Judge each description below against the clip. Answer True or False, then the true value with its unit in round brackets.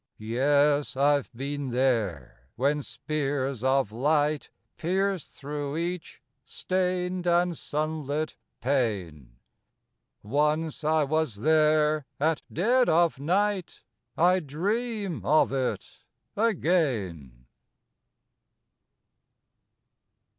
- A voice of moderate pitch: True (150 Hz)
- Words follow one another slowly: True (80 wpm)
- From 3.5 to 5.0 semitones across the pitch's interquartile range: True (4.3 semitones)